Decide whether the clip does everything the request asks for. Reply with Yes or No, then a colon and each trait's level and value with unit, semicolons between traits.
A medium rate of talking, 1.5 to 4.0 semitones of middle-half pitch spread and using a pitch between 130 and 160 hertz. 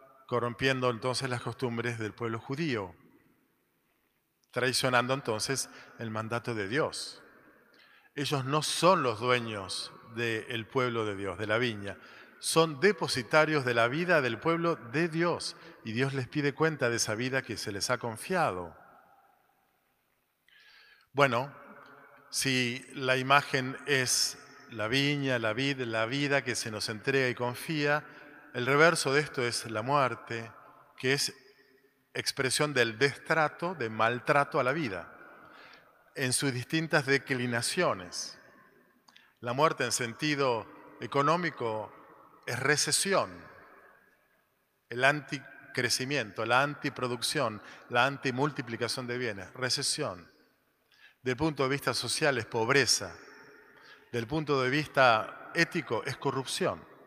No: slow, 120 wpm; average, 3.4 semitones; low, 135 Hz